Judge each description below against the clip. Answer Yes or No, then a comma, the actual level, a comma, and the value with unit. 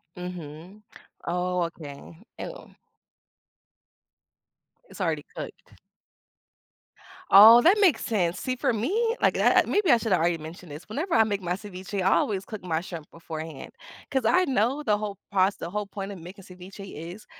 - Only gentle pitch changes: No, average, 4.2 semitones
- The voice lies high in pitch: Yes, high, 195 Hz